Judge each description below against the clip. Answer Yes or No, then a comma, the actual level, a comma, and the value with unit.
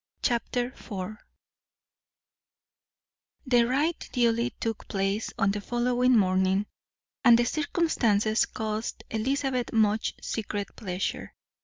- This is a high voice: Yes, high, 225 Hz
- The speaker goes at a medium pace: No, slow, 100 wpm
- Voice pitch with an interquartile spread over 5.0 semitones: No, average, 3.2 semitones